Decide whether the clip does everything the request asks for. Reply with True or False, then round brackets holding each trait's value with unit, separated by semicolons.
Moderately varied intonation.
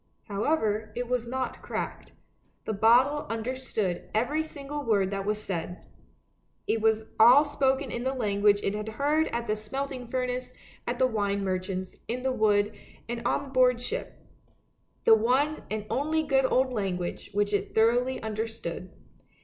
True (3.9 semitones)